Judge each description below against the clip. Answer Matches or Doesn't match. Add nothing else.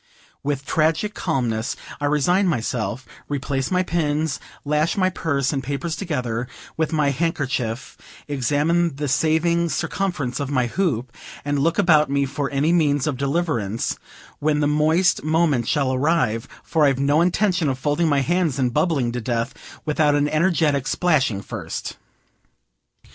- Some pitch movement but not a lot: Matches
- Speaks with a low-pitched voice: Doesn't match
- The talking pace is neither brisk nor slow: Matches